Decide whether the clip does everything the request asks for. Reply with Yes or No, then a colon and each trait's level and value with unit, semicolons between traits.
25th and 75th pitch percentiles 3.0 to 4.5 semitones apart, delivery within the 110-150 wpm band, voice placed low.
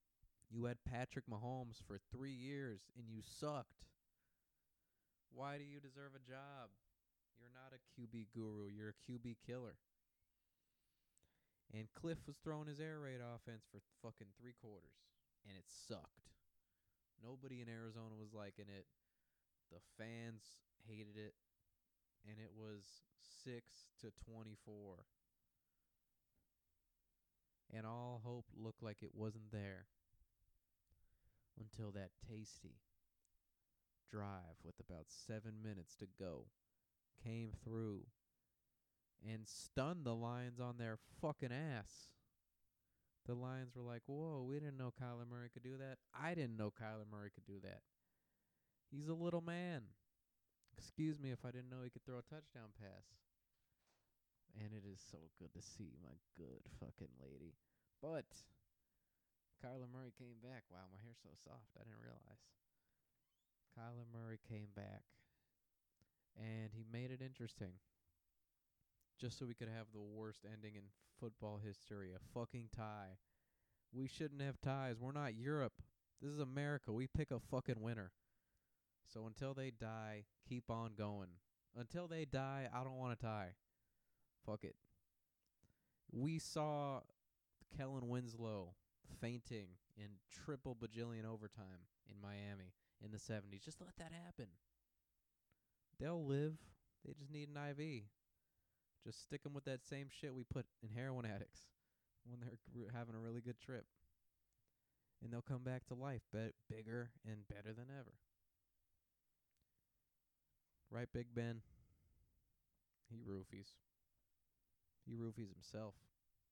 Yes: average, 3.8 semitones; slow, 135 wpm; low, 115 Hz